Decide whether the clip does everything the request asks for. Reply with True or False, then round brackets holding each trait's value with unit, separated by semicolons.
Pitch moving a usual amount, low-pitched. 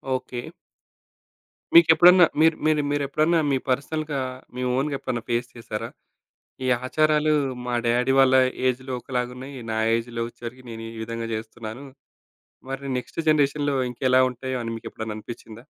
True (3.6 semitones; 130 Hz)